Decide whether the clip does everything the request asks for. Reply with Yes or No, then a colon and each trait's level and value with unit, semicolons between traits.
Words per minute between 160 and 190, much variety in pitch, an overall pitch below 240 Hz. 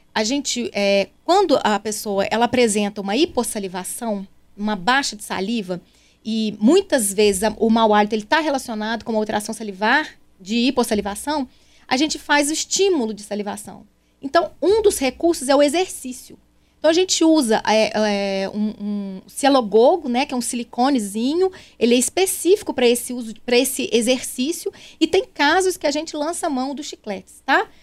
No: average, 170 wpm; wide, 6.1 semitones; high, 245 Hz